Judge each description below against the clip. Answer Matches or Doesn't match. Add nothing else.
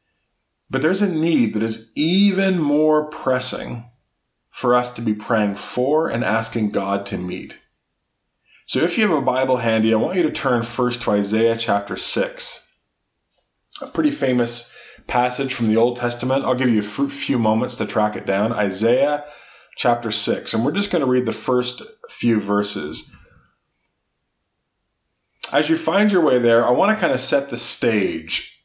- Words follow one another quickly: Doesn't match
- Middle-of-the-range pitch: Doesn't match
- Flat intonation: Doesn't match